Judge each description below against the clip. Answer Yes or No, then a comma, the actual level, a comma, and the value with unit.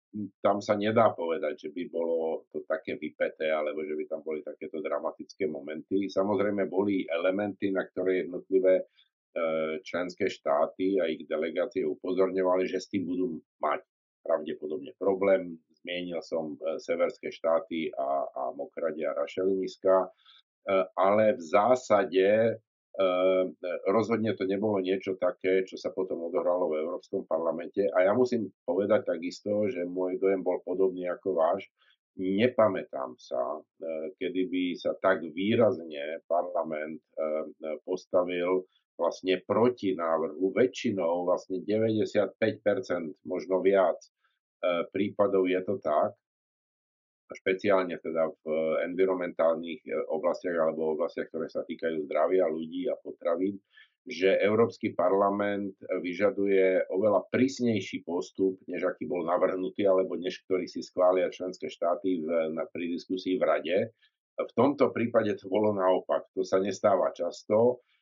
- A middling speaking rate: Yes, average, 130 wpm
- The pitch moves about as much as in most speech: No, narrow, 2.2 semitones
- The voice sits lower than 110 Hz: Yes, very low, 95 Hz